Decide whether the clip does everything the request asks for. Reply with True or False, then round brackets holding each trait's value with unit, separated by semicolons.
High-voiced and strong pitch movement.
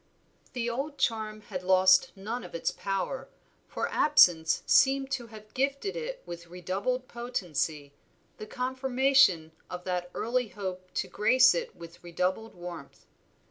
True (215 Hz; 6.0 semitones)